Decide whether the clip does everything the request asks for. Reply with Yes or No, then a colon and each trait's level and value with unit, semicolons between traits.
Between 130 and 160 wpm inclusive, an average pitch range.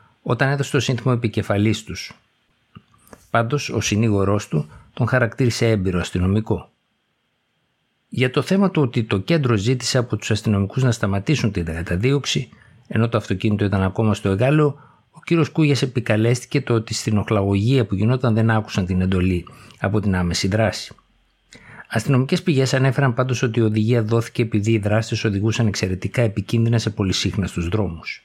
Yes: average, 150 wpm; average, 3.9 semitones